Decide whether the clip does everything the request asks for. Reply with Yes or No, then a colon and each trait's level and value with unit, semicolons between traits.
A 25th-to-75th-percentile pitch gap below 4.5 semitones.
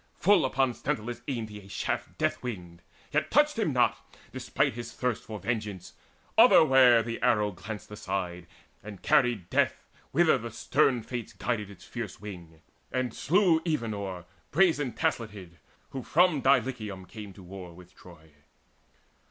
No: average, 4.9 semitones